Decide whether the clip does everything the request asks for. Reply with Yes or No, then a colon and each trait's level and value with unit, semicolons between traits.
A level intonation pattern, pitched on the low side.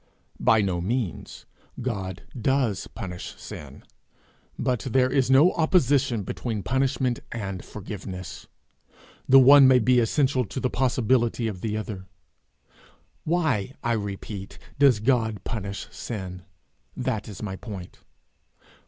No: average, 4.8 semitones; low, 115 Hz